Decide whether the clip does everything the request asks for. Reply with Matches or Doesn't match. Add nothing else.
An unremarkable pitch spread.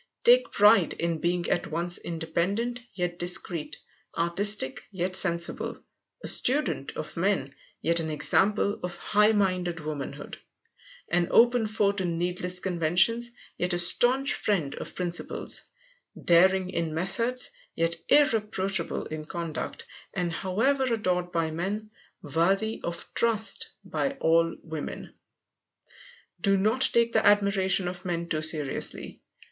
Matches